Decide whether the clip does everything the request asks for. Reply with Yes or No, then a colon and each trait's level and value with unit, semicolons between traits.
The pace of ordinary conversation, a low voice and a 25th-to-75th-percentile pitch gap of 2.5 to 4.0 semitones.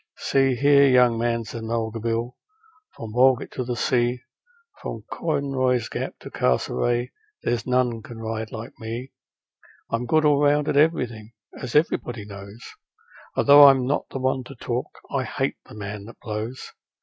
Yes: average, 160 wpm; low, 120 Hz; average, 2.8 semitones